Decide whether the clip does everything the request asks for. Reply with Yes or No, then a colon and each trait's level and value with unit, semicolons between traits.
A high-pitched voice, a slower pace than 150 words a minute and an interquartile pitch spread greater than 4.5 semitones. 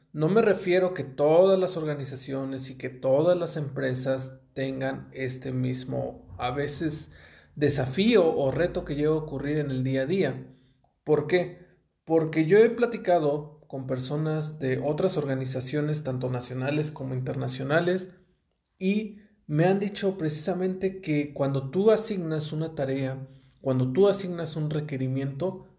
No: medium, 150 Hz; average, 140 wpm; average, 5.1 semitones